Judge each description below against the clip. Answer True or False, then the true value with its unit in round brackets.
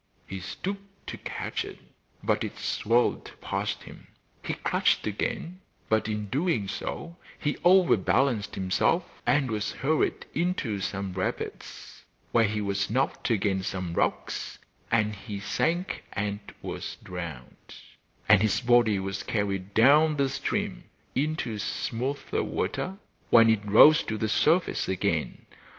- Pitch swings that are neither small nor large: False (6.5 semitones)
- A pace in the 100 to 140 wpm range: True (135 wpm)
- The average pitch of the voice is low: True (110 Hz)